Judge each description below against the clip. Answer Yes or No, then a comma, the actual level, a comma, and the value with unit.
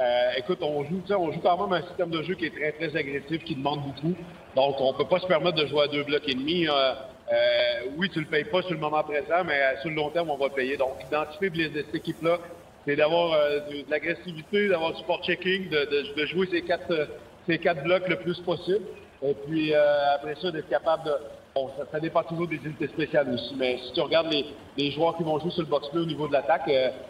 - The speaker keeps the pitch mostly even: No, average, 3.2 semitones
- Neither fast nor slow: No, fast, 260 wpm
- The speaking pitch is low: No, medium, 155 Hz